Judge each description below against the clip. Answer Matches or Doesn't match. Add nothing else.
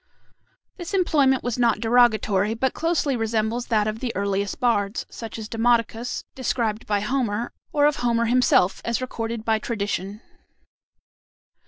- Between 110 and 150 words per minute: Matches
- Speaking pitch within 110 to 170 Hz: Doesn't match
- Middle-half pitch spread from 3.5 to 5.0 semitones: Doesn't match